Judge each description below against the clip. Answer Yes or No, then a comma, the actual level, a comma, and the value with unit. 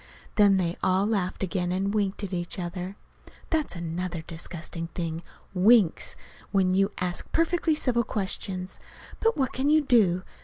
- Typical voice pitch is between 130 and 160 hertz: No, high, 190 Hz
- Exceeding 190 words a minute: No, average, 155 wpm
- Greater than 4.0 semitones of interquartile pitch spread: No, average, 3.7 semitones